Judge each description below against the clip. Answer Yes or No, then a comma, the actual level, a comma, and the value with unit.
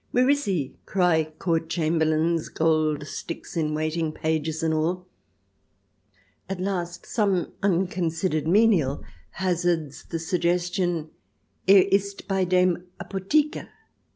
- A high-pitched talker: No, medium, 170 Hz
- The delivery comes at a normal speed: No, slow, 125 wpm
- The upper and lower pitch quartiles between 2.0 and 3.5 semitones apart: Yes, average, 3.0 semitones